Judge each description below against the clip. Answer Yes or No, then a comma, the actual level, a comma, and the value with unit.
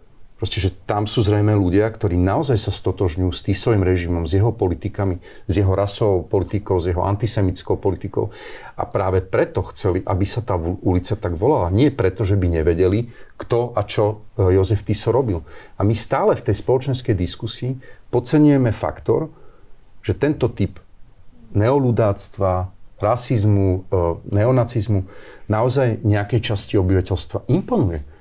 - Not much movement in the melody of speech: No, average, 3.6 semitones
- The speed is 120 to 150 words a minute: Yes, average, 140 wpm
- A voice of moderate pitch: No, low, 105 Hz